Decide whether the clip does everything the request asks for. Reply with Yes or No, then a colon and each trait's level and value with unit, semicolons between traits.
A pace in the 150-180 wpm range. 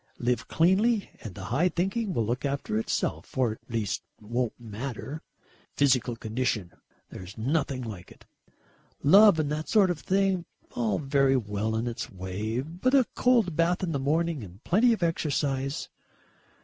Yes: average, 160 wpm